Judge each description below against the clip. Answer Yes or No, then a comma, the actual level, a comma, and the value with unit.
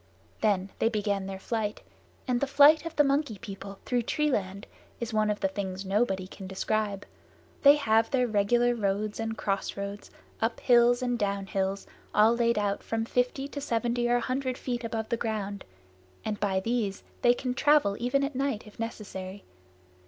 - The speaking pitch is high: Yes, high, 225 Hz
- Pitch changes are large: No, average, 3.5 semitones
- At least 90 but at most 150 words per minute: No, average, 175 wpm